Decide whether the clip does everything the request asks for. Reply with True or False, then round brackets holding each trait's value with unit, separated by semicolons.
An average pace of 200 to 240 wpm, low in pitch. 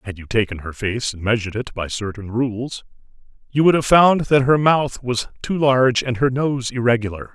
True (205 wpm; 120 Hz)